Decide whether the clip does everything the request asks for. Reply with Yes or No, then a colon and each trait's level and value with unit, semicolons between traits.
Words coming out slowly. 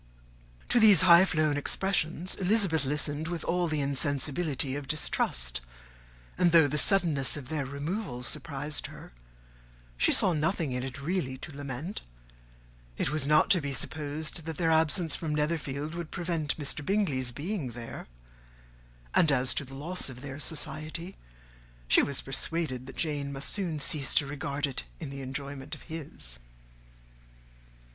No: average, 155 wpm